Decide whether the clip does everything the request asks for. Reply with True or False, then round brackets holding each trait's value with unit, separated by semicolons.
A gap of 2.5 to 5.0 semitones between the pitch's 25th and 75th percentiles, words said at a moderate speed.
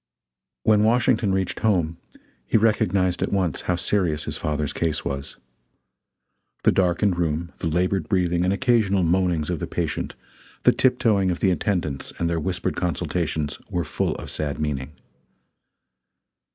True (3.7 semitones; 150 wpm)